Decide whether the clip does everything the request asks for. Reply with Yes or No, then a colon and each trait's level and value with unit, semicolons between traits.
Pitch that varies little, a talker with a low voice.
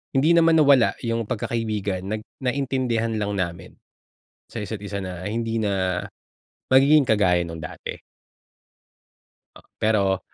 No: average, 4.4 semitones; low, 110 Hz